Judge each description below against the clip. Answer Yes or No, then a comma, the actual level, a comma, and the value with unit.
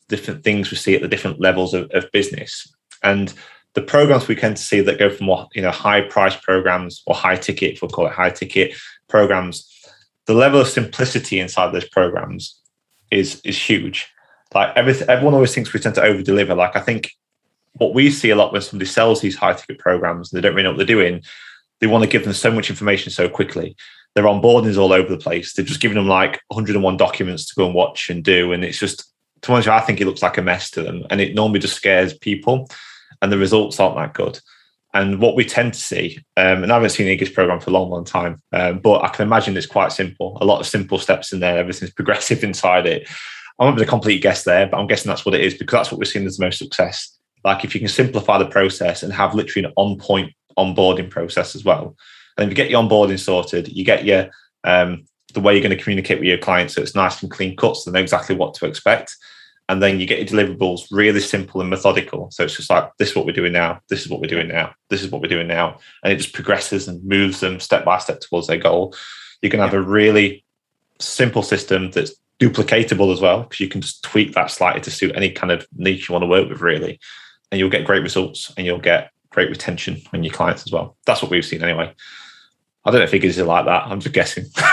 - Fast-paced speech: Yes, fast, 245 wpm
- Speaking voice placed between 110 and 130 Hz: No, low, 100 Hz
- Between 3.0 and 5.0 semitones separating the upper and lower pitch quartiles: No, narrow, 2.6 semitones